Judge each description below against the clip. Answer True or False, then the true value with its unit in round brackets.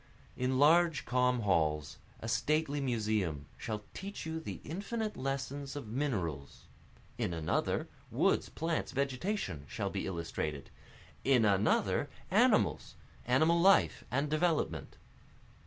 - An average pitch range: False (7.6 semitones)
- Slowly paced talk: True (115 wpm)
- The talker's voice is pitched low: True (130 Hz)